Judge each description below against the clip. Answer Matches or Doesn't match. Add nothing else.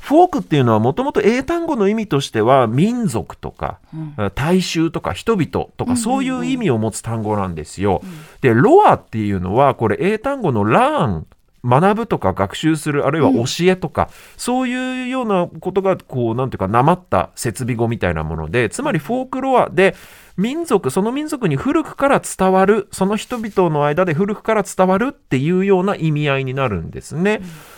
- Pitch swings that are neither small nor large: Doesn't match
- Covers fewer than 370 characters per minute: Doesn't match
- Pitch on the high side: Doesn't match